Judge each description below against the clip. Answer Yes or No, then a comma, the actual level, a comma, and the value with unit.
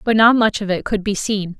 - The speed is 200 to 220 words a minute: No, fast, 300 wpm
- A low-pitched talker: No, high, 205 Hz